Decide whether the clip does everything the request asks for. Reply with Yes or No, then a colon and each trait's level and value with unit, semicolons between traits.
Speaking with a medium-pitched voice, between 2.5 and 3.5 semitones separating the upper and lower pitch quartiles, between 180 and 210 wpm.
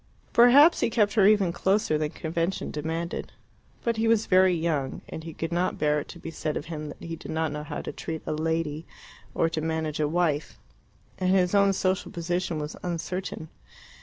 Yes: medium, 165 Hz; average, 3.2 semitones; average, 200 wpm